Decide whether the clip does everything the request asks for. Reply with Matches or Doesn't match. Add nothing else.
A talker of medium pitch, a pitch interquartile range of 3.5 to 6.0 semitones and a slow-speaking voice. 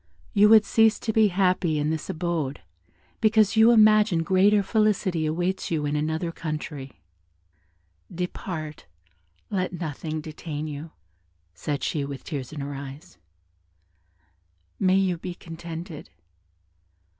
Matches